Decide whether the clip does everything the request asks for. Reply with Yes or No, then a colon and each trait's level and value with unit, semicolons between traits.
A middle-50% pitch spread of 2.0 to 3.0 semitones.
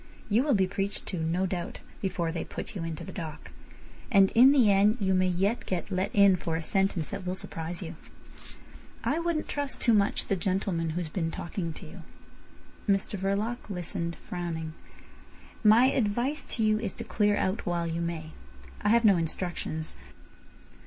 No: average, 3.7 semitones